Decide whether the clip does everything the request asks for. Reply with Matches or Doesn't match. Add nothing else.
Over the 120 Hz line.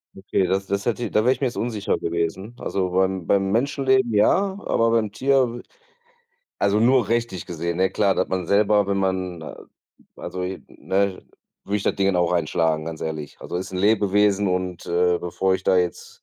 Doesn't match